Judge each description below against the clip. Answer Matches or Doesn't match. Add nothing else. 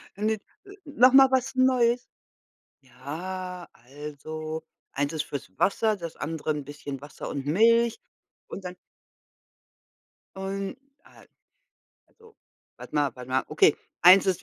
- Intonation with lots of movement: Matches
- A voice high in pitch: Doesn't match